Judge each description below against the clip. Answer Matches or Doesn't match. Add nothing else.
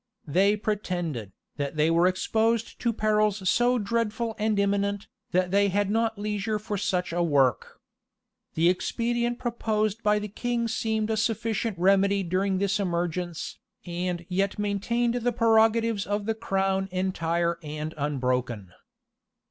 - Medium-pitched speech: Doesn't match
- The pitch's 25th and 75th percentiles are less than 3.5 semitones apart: Doesn't match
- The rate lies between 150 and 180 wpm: Doesn't match